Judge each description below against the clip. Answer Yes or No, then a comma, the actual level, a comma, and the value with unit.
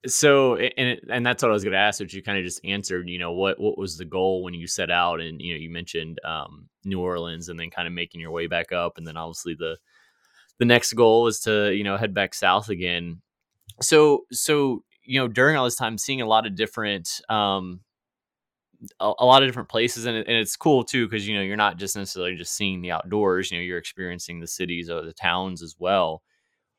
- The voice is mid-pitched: No, very low, 95 Hz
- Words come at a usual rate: No, fast, 240 wpm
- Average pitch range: Yes, average, 4.6 semitones